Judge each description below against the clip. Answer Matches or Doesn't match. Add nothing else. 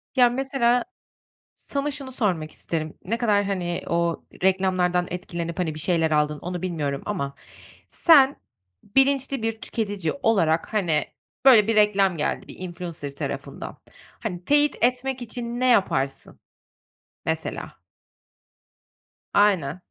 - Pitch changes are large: Matches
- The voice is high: Matches